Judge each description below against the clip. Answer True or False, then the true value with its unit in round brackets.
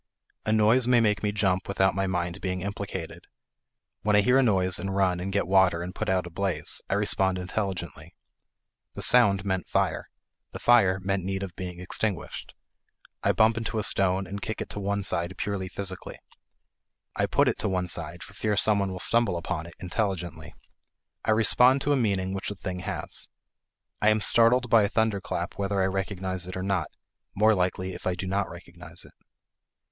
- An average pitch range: False (2.2 semitones)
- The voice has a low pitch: True (95 Hz)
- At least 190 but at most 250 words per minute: True (195 wpm)